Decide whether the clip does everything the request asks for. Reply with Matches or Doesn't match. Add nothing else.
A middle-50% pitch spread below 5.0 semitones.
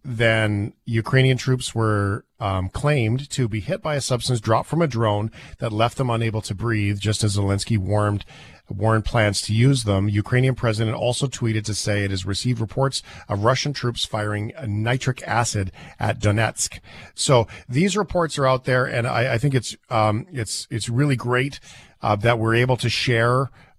Matches